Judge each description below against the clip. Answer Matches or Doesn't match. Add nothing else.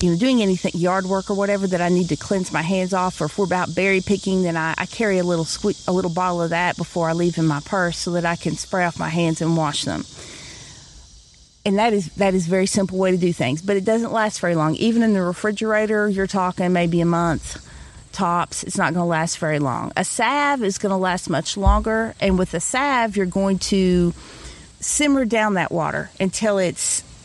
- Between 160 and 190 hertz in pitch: Matches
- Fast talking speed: Matches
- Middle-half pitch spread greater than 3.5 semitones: Doesn't match